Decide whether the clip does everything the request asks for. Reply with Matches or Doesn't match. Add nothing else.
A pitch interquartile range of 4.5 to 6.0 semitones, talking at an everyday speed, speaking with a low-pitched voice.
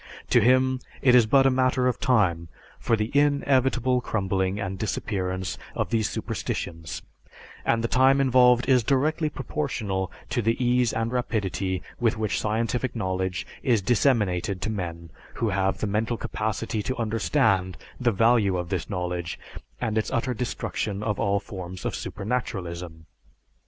Matches